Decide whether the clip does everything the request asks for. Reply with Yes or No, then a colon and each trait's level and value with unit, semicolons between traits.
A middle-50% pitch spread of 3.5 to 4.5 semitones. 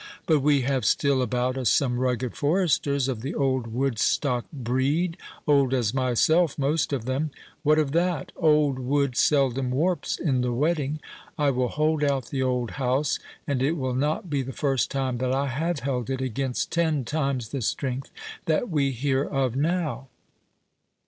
No: average, 2.7 semitones